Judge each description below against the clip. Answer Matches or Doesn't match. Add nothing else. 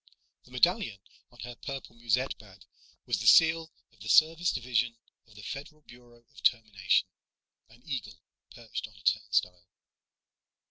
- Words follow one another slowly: Doesn't match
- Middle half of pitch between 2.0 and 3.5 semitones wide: Doesn't match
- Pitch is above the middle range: Doesn't match